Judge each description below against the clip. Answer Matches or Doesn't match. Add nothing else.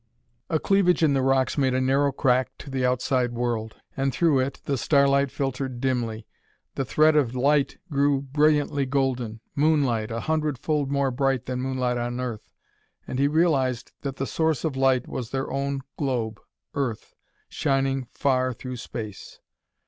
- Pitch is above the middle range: Doesn't match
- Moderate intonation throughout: Doesn't match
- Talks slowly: Doesn't match